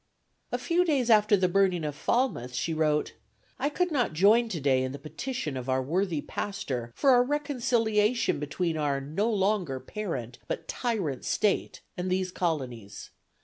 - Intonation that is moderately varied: No, wide, 8.1 semitones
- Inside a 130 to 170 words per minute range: Yes, average, 160 wpm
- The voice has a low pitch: No, medium, 185 Hz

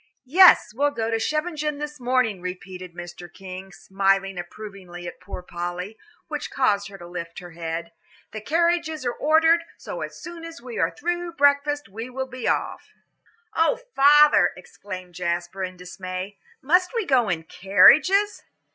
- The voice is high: Yes, high, 215 Hz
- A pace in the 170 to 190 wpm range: No, average, 155 wpm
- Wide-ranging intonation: Yes, wide, 8.4 semitones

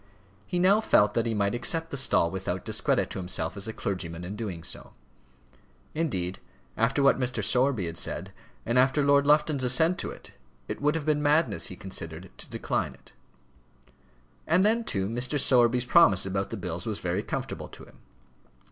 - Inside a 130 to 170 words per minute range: No, average, 185 wpm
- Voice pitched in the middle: No, low, 120 Hz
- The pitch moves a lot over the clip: Yes, wide, 7.4 semitones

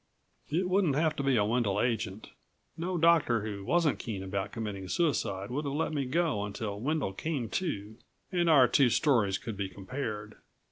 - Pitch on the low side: Yes, low, 120 Hz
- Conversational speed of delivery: Yes, average, 180 wpm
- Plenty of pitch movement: Yes, wide, 7.2 semitones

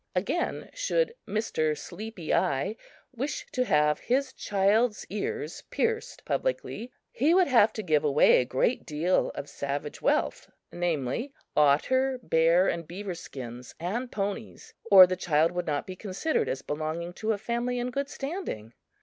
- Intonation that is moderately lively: No, wide, 8.2 semitones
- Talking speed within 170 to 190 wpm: No, average, 150 wpm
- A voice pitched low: No, high, 195 Hz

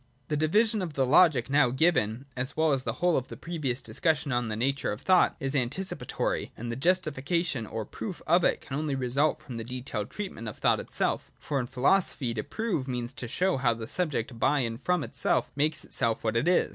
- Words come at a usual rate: No, fast, 220 wpm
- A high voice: No, low, 135 Hz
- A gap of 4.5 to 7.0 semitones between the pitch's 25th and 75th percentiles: Yes, average, 5.1 semitones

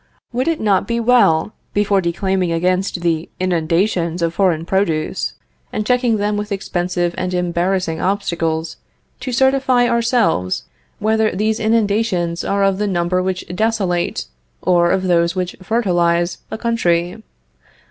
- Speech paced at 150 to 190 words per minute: No, slow, 135 wpm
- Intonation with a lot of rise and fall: No, average, 4.0 semitones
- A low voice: No, medium, 185 Hz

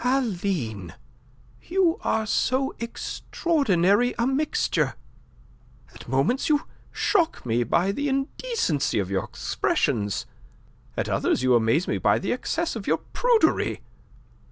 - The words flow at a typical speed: No, slow, 120 wpm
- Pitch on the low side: No, high, 230 Hz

